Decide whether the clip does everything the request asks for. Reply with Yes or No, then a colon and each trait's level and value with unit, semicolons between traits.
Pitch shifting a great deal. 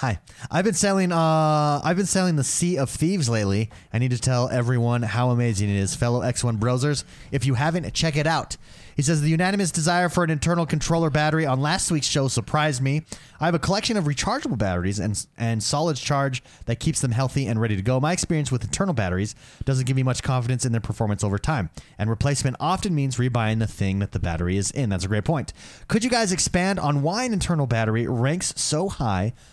Yes: wide, 5.9 semitones